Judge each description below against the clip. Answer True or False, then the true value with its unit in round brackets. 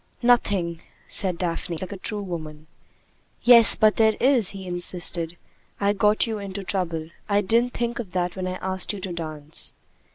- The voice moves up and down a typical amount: True (3.6 semitones)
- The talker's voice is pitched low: False (190 Hz)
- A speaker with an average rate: True (170 wpm)